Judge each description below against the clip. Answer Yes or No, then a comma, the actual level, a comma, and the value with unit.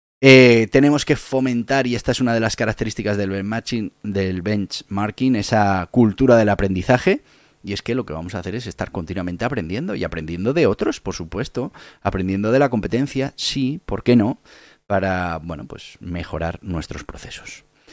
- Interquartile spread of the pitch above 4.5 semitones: Yes, average, 4.9 semitones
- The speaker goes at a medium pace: Yes, average, 170 wpm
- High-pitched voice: No, low, 110 Hz